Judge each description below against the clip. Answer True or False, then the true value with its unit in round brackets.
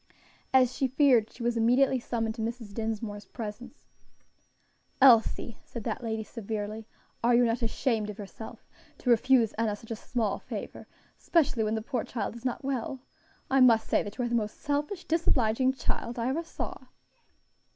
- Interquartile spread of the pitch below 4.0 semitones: True (2.7 semitones)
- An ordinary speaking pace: True (170 wpm)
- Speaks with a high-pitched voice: True (235 Hz)